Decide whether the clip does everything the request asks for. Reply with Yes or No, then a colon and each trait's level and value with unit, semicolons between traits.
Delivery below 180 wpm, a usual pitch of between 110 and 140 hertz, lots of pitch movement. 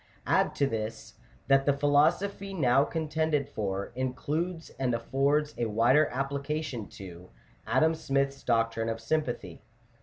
No: average, 140 wpm; low, 135 Hz; average, 4.9 semitones